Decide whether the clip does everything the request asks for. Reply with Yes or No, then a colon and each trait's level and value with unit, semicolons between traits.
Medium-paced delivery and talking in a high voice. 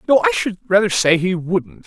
No: fast, 225 wpm; high, 200 Hz